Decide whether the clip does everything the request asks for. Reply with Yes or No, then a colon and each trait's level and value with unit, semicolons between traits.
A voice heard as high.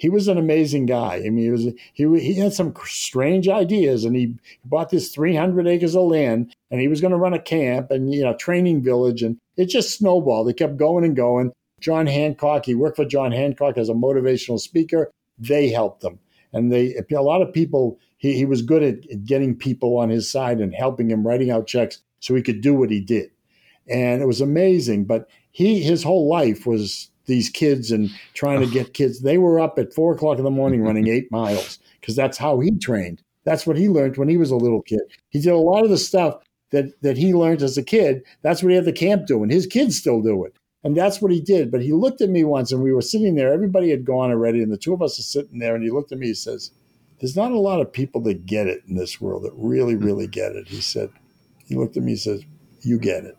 No: low, 135 Hz